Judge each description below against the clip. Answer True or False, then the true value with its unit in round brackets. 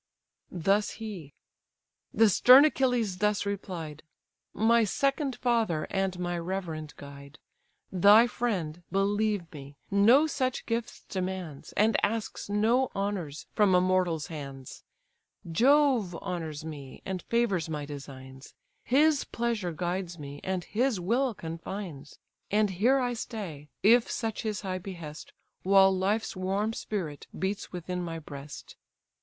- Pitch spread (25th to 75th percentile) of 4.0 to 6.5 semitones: True (5.4 semitones)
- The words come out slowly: True (125 wpm)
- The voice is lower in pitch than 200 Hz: True (190 Hz)